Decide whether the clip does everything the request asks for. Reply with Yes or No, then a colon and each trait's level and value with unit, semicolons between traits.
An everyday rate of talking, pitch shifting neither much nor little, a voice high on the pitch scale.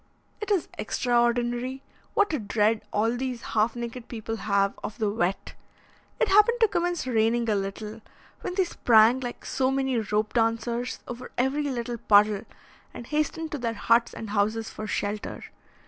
Yes: average, 160 wpm; average, 3.3 semitones; high, 235 Hz